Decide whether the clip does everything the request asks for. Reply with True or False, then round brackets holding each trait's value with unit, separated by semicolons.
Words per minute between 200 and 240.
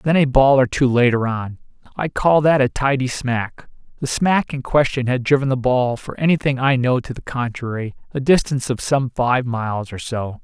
True (205 wpm)